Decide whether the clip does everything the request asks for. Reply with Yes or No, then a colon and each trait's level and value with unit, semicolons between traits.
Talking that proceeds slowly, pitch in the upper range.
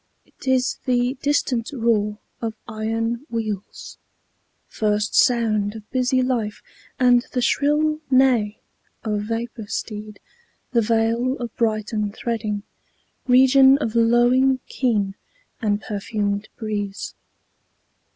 Yes: slow, 105 wpm; high, 230 Hz